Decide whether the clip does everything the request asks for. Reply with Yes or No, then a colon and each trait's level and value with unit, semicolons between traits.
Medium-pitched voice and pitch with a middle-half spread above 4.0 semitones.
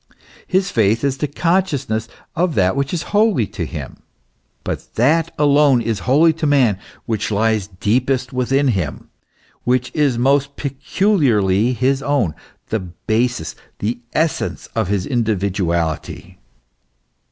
No: low, 125 Hz; average, 5.1 semitones